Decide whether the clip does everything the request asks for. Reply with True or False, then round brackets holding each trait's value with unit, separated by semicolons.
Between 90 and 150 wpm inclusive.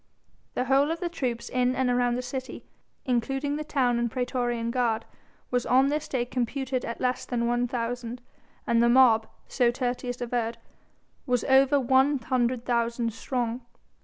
False (160 wpm)